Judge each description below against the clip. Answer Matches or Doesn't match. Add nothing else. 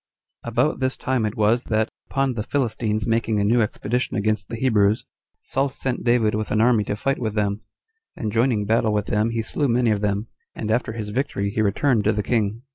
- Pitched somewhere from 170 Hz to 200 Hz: Doesn't match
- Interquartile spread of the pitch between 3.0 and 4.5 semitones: Doesn't match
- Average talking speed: Doesn't match